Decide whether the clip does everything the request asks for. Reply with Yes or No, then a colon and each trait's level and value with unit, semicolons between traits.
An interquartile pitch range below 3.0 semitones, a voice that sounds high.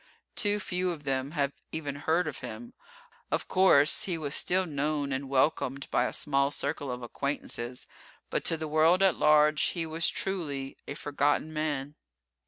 No: narrow, 2.6 semitones; medium, 150 Hz